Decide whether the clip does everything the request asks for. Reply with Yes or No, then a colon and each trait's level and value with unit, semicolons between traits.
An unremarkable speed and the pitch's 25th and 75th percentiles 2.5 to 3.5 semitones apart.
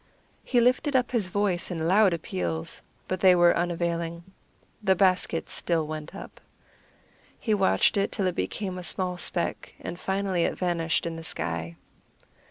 Yes: average, 160 wpm; average, 2.8 semitones